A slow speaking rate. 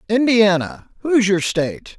Yes: slow, 90 wpm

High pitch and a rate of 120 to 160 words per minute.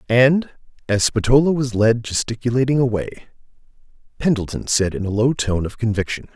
No: low, 120 Hz; average, 140 wpm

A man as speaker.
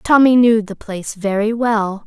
No: female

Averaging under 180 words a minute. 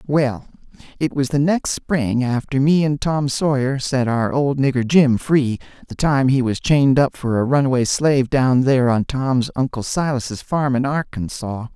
No: average, 185 wpm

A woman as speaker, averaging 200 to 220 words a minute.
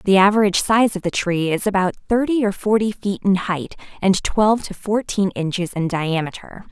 No: female; average, 190 wpm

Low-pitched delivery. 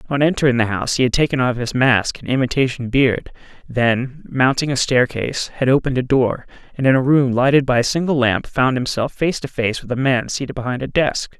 Yes: low, 130 Hz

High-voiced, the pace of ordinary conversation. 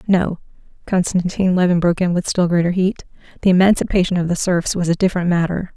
No: medium, 180 Hz; average, 190 wpm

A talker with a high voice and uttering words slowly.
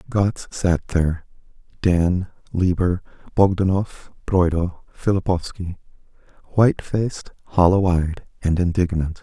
No: very low, 90 Hz; slow, 85 wpm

